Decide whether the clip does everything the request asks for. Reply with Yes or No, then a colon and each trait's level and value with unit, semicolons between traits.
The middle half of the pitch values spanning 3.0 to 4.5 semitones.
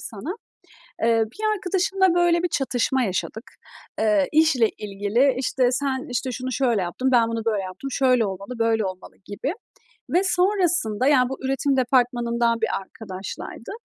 Yes: average, 3.9 semitones